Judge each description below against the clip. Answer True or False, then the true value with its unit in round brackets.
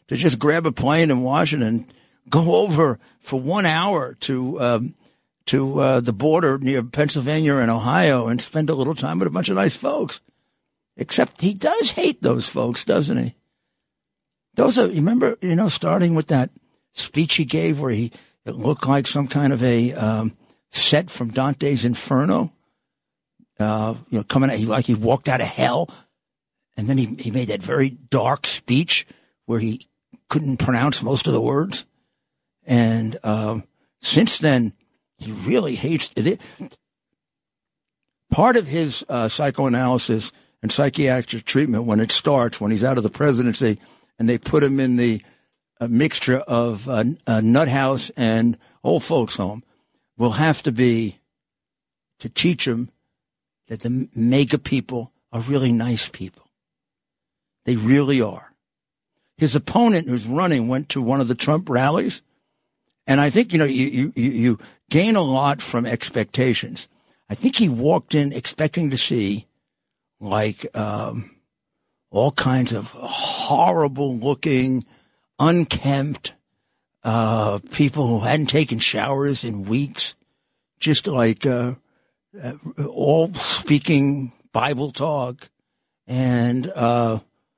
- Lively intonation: False (3.8 semitones)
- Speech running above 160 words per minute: False (145 wpm)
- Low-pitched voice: True (130 Hz)